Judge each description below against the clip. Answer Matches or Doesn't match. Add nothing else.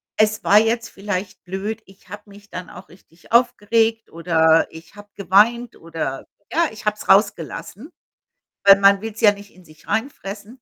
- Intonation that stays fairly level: Doesn't match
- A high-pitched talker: Matches